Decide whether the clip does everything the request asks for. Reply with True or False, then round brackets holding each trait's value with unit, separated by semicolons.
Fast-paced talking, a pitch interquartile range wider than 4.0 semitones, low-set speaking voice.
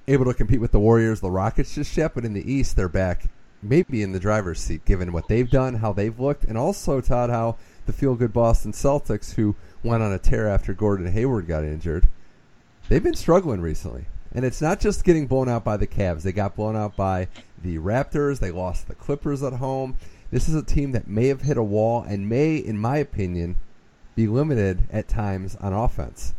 True (215 wpm; 5.5 semitones; 110 Hz)